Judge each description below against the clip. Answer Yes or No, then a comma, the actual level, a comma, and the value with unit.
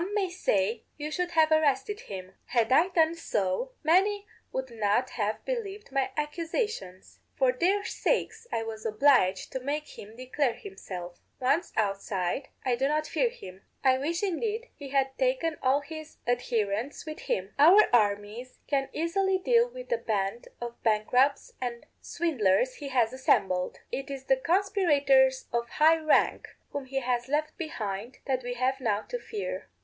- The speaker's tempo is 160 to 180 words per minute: Yes, average, 165 wpm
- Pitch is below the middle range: No, very high, 270 Hz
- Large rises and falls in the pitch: Yes, wide, 6.3 semitones